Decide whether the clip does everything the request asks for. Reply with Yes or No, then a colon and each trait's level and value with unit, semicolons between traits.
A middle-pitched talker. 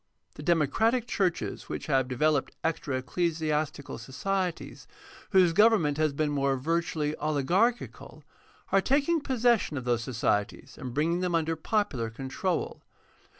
Yes: medium, 160 Hz